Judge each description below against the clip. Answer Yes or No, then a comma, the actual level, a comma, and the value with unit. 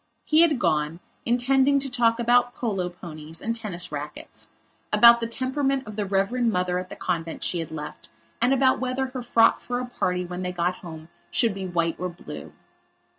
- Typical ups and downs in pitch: No, wide, 5.8 semitones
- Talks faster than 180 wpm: Yes, average, 190 wpm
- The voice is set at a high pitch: Yes, high, 215 Hz